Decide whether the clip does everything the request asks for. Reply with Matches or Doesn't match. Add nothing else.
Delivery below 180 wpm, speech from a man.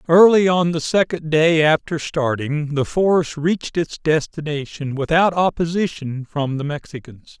Matches